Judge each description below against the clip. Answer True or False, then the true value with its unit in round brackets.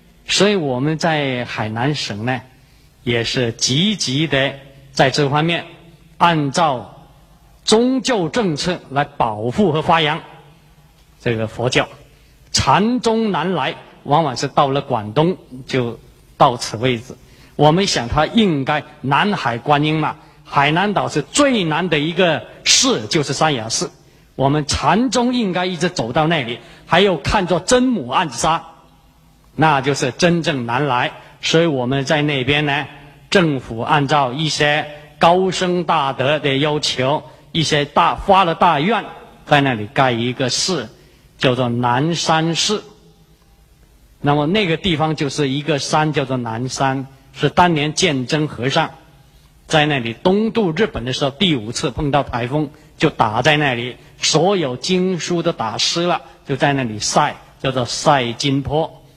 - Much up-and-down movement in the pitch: False (3.8 semitones)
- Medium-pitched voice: True (150 Hz)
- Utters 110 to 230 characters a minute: True (210 characters per minute)